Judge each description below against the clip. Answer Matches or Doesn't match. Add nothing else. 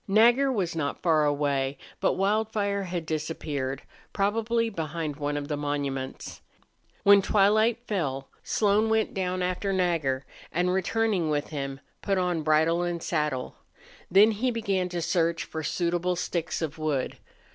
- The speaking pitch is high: Doesn't match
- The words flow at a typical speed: Matches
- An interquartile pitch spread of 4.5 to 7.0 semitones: Matches